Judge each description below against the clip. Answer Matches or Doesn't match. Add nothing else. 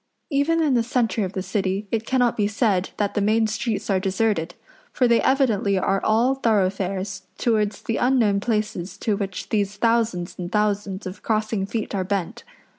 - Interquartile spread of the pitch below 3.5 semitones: Matches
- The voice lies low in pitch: Doesn't match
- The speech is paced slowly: Doesn't match